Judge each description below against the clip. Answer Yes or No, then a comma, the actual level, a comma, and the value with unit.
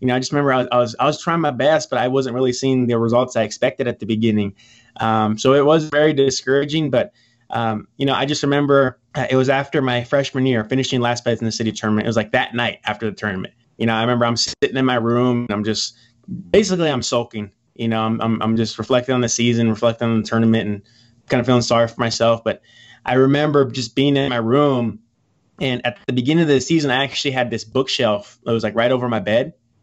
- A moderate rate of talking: No, fast, 245 wpm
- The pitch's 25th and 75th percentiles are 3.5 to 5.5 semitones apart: No, average, 3.0 semitones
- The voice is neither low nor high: No, low, 120 Hz